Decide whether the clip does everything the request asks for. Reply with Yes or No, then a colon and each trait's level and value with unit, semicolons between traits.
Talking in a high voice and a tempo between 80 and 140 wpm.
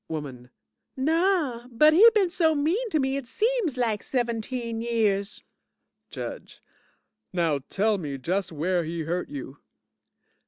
Yes: high, 230 Hz; slow, 135 wpm